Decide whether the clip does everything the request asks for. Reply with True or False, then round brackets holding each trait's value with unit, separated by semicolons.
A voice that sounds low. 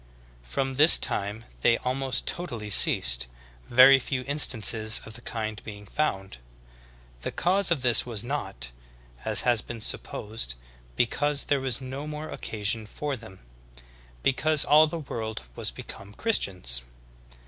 True (120 Hz)